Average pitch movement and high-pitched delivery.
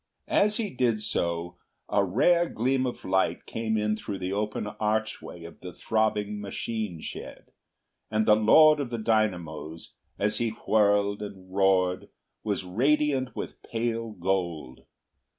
No: average, 3.4 semitones; low, 105 Hz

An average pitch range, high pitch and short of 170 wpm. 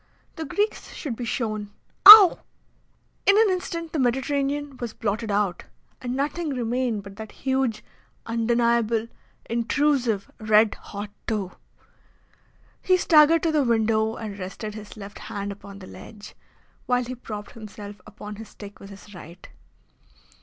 Yes: average, 4.4 semitones; high, 230 Hz; average, 140 wpm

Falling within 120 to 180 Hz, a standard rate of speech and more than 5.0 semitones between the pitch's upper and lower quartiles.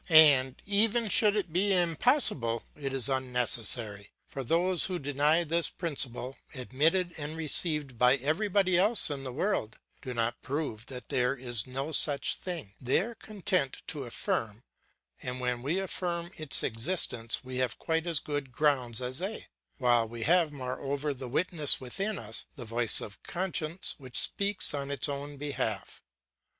Yes: medium, 140 Hz; average, 160 wpm; wide, 5.5 semitones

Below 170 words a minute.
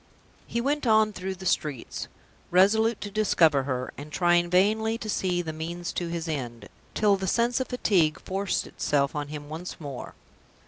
No: average, 175 wpm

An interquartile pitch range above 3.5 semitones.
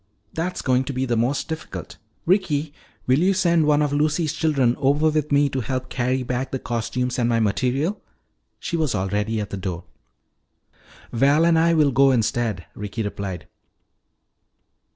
Yes: average, 4.6 semitones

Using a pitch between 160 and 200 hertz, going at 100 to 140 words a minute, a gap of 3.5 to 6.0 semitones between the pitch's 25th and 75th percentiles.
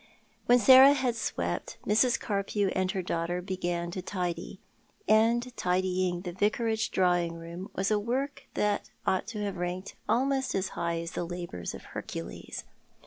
No: high, 190 Hz; average, 155 wpm; average, 4.0 semitones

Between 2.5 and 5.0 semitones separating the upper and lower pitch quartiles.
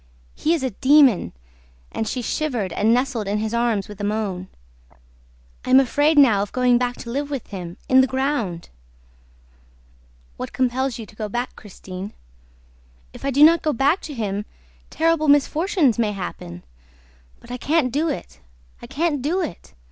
No: wide, 5.6 semitones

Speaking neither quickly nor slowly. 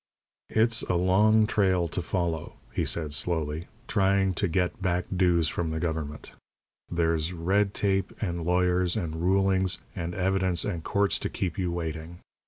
Yes: average, 155 wpm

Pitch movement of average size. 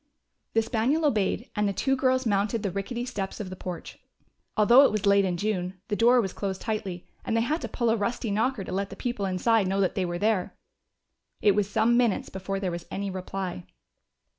Yes: average, 3.4 semitones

